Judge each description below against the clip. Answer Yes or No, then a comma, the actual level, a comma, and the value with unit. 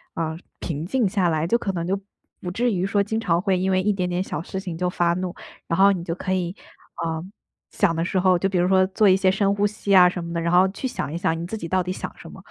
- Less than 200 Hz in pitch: Yes, medium, 185 Hz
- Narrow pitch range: Yes, narrow, 2.3 semitones